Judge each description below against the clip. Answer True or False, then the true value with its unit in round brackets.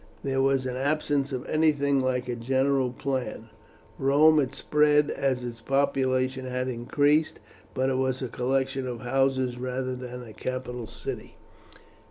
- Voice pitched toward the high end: False (130 Hz)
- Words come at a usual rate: True (150 wpm)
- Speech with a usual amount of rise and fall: False (1.5 semitones)